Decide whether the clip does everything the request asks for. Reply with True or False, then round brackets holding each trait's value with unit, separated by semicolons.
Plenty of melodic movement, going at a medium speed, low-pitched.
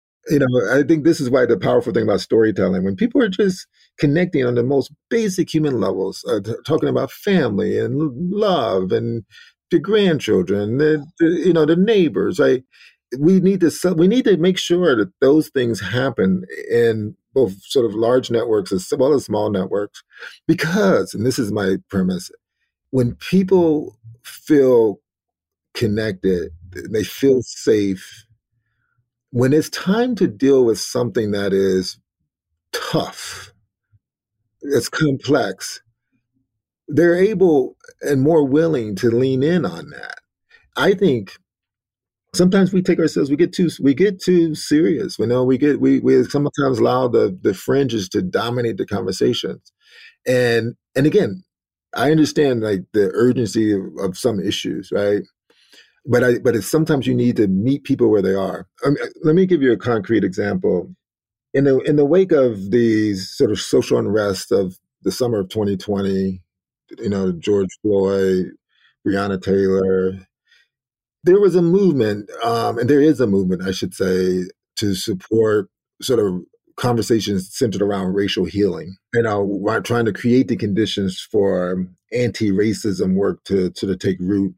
True (7.7 semitones; 155 wpm; 120 Hz)